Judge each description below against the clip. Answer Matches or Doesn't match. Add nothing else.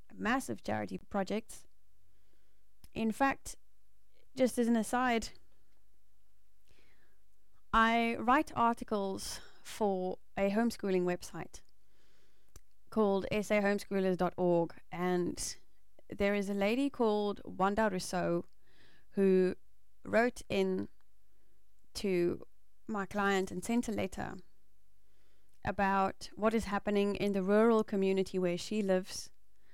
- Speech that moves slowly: Matches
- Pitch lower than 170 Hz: Doesn't match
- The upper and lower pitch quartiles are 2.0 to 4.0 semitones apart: Matches